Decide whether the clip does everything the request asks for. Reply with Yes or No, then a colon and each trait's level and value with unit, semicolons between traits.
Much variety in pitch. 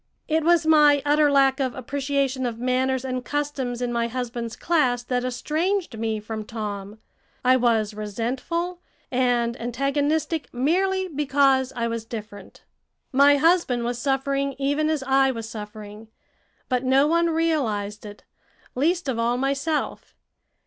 No: average, 3.8 semitones